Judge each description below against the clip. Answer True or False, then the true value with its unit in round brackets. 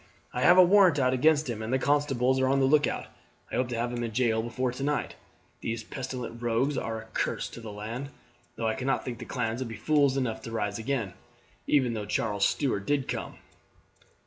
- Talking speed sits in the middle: False (215 wpm)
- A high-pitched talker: False (125 Hz)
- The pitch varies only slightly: False (3.3 semitones)